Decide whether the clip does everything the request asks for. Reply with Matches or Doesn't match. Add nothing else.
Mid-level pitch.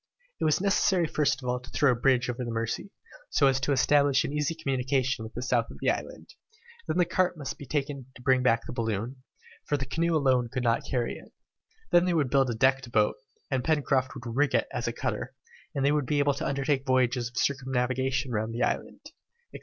Doesn't match